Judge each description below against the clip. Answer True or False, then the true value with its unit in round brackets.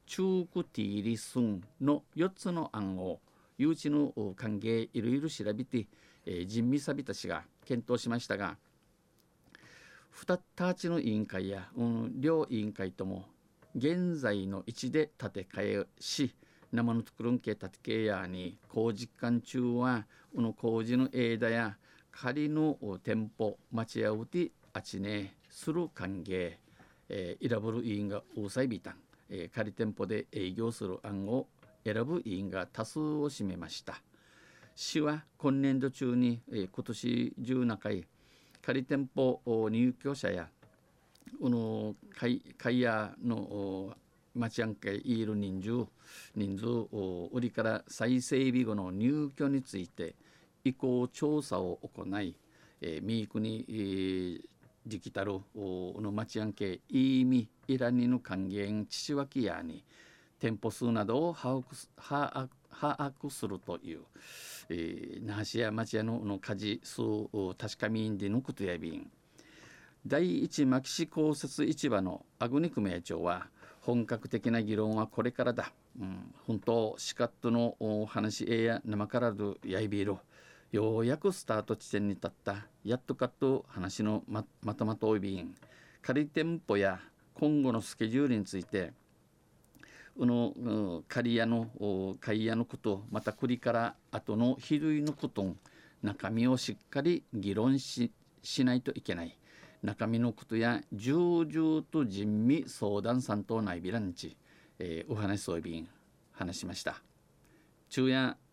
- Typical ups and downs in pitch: True (4.0 semitones)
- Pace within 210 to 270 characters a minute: True (240 characters per minute)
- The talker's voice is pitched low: True (115 Hz)